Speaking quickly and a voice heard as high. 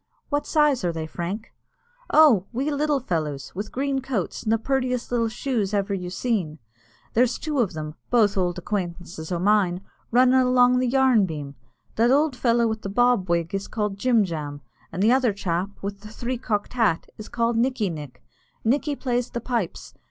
No: average, 185 wpm; high, 220 Hz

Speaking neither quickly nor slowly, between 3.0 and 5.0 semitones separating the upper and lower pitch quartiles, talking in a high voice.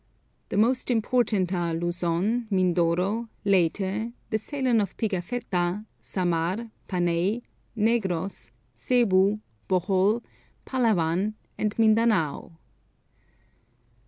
No: slow, 80 wpm; average, 4.3 semitones; high, 200 Hz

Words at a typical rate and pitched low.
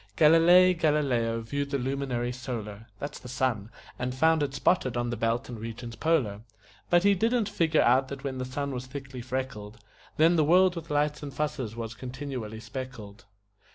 Yes: average, 180 wpm; low, 130 Hz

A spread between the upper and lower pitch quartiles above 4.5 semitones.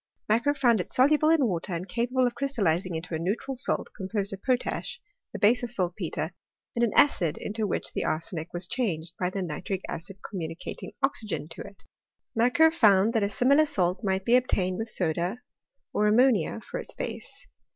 Yes: wide, 5.5 semitones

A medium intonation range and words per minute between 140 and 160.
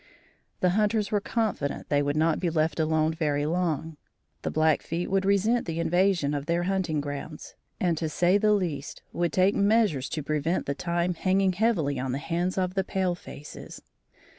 No: average, 3.8 semitones; average, 180 wpm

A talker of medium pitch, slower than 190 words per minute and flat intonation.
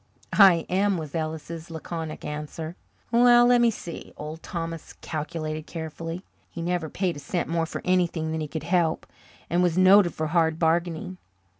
Yes: medium, 165 Hz; average, 160 wpm; narrow, 2.2 semitones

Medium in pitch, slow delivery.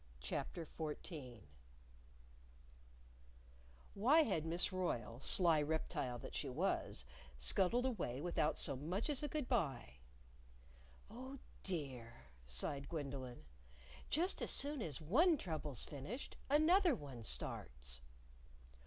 Yes: medium, 160 Hz; slow, 110 wpm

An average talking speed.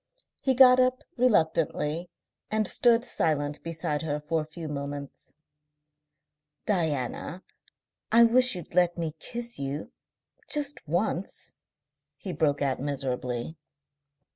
No: slow, 115 wpm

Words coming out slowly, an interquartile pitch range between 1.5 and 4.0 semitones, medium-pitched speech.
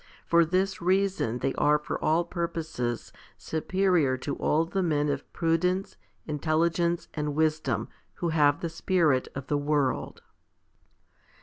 Yes: slow, 130 wpm; average, 2.8 semitones; medium, 160 Hz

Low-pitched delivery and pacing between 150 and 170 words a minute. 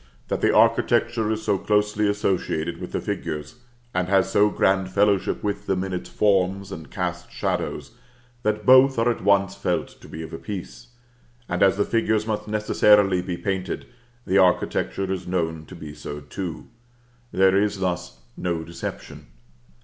Yes: very low, 95 Hz; average, 165 wpm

